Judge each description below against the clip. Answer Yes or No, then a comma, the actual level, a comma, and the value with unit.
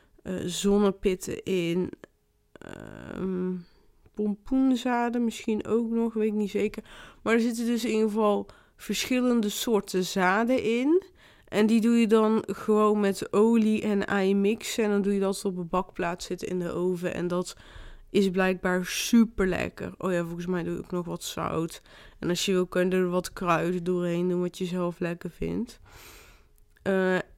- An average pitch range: Yes, average, 3.3 semitones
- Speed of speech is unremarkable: Yes, average, 170 wpm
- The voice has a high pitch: Yes, high, 195 Hz